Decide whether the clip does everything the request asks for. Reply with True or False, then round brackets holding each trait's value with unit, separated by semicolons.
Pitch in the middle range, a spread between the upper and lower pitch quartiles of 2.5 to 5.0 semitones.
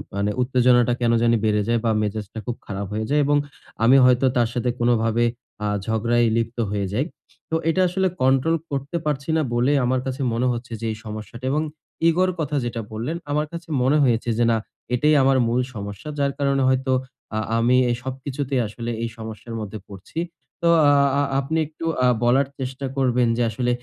False (125 Hz; 3.2 semitones)